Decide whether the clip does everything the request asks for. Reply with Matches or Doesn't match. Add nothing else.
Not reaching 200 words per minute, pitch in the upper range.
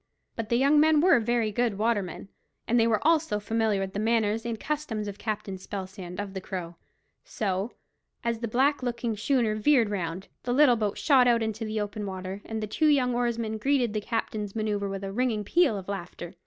Doesn't match